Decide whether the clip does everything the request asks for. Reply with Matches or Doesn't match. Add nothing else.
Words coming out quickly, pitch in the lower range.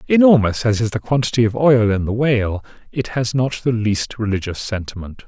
Doesn't match